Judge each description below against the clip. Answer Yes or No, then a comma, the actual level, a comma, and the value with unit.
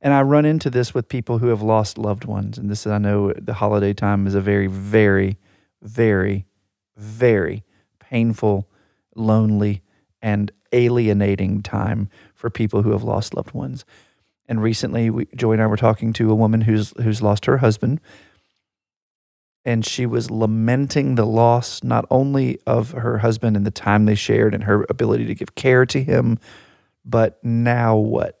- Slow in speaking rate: No, average, 170 wpm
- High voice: No, low, 110 Hz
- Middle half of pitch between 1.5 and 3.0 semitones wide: Yes, narrow, 2.5 semitones